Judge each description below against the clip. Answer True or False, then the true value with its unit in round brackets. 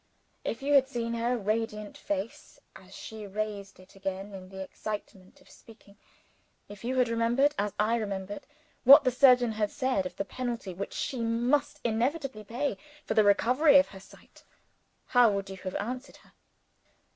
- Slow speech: False (170 wpm)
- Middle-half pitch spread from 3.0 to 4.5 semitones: True (3.9 semitones)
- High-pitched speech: True (225 Hz)